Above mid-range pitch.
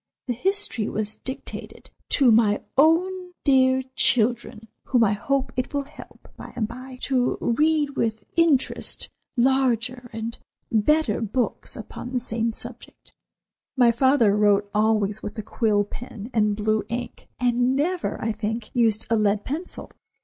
Yes: high, 240 Hz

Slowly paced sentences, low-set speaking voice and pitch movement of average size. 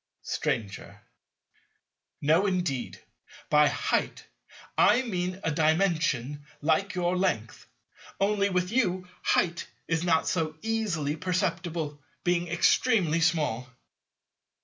No: slow, 100 wpm; medium, 170 Hz; average, 3.4 semitones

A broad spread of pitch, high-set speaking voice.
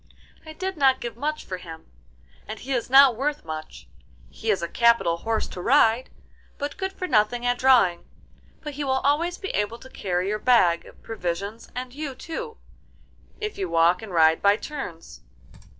Yes: wide, 7.3 semitones; high, 235 Hz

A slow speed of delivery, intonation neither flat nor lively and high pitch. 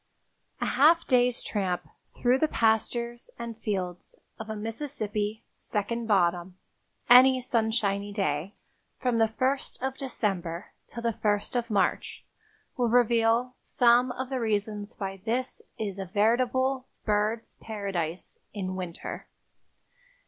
Yes: slow, 125 wpm; average, 3.4 semitones; high, 220 Hz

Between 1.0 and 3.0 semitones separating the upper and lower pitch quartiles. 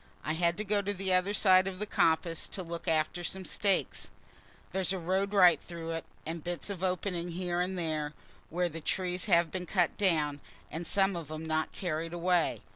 Yes: narrow, 2.4 semitones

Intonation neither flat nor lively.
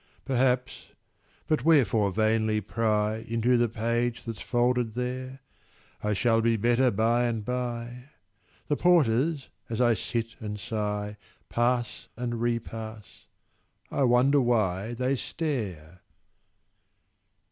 No: narrow, 2.3 semitones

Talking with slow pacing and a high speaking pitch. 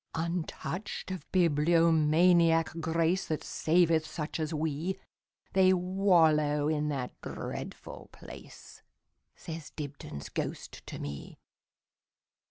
No: slow, 80 wpm; medium, 160 Hz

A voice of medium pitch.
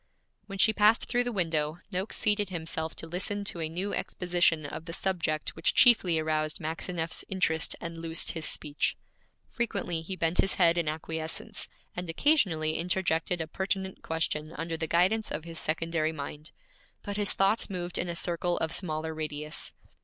Yes: medium, 170 Hz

